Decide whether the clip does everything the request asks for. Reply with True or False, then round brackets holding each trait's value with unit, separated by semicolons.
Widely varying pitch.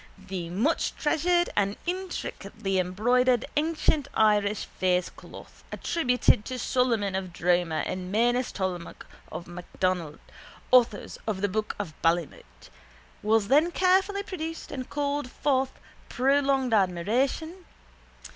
True (7.3 semitones)